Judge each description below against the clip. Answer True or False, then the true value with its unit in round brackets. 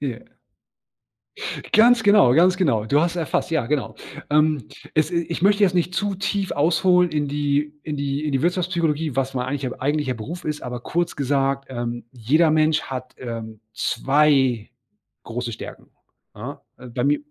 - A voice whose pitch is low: False (145 Hz)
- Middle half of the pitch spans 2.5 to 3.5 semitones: False (4.7 semitones)